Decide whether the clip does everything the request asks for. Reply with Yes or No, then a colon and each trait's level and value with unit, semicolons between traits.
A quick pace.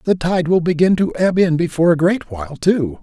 Yes: fast, 240 wpm